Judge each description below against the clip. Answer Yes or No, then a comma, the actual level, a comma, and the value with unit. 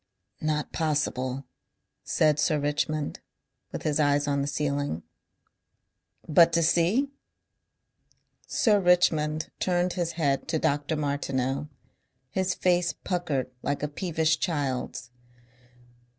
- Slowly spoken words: Yes, slow, 110 wpm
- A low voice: No, medium, 150 Hz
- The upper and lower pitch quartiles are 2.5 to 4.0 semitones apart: Yes, average, 3.1 semitones